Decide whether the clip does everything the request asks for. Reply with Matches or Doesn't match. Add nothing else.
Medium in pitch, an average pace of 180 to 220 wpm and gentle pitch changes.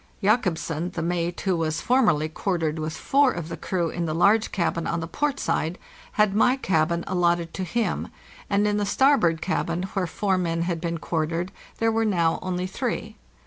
Doesn't match